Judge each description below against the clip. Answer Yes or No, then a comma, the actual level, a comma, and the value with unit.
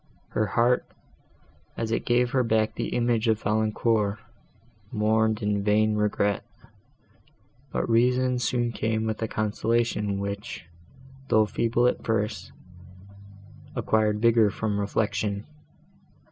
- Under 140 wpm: Yes, slow, 115 wpm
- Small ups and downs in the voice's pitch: Yes, narrow, 1.8 semitones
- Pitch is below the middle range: Yes, low, 110 Hz